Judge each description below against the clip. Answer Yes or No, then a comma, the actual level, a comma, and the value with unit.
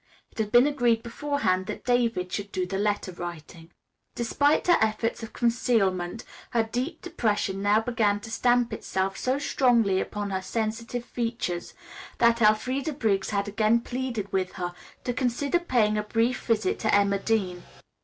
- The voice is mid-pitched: No, high, 225 Hz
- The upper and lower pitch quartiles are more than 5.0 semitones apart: No, average, 3.6 semitones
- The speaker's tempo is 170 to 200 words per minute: No, average, 160 wpm